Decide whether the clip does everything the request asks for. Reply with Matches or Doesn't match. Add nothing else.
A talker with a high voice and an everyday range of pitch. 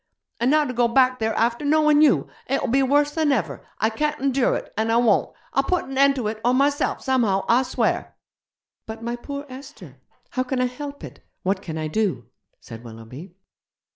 Matches